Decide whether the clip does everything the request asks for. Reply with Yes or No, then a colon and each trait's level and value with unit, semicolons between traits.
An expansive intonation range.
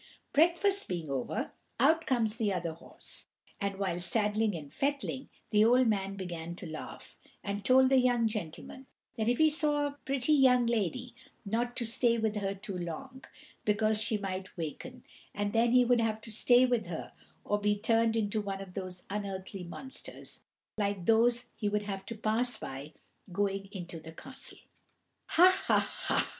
No: average, 4.2 semitones